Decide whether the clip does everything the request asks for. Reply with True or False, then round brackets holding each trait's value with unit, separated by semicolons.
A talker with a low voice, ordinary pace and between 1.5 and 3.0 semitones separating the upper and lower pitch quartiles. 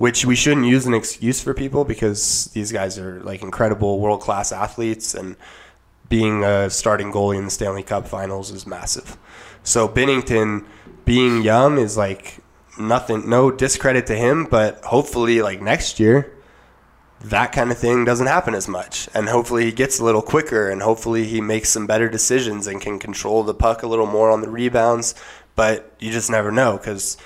True (110 Hz; 185 wpm; 2.7 semitones)